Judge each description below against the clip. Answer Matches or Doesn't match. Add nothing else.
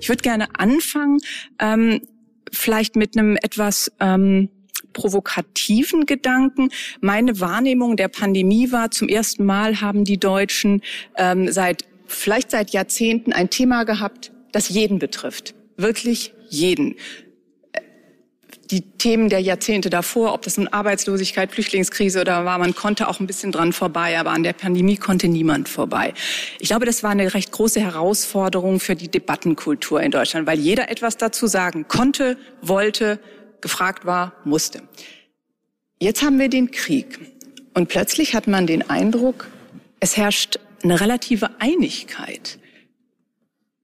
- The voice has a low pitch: Doesn't match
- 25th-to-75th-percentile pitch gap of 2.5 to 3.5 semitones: Doesn't match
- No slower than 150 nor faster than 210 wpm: Doesn't match